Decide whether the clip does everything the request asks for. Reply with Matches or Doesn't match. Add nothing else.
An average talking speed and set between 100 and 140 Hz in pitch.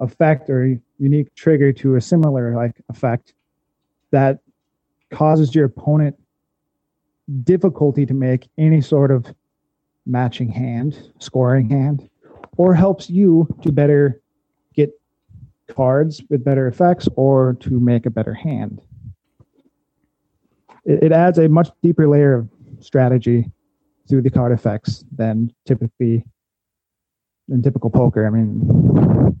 Doesn't match